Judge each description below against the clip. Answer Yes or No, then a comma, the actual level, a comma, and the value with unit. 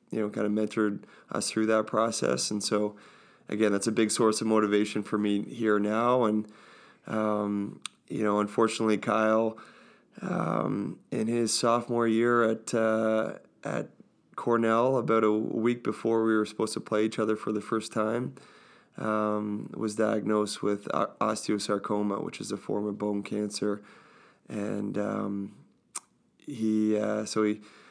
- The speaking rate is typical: Yes, average, 150 wpm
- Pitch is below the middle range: Yes, low, 110 Hz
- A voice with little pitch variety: Yes, narrow, 1.1 semitones